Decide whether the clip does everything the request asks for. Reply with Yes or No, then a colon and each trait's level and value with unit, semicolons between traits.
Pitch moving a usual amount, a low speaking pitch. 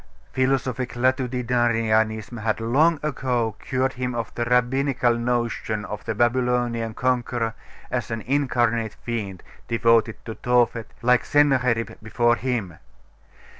No: narrow, 2.0 semitones; low, 120 Hz